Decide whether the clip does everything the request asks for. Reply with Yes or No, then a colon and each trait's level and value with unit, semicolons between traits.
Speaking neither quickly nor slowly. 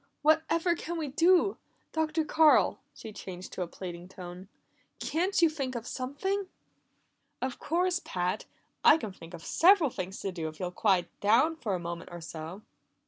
Yes: average, 175 wpm